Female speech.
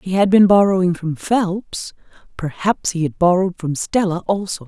Yes: female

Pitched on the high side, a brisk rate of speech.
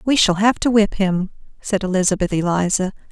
No: high, 195 Hz; average, 175 wpm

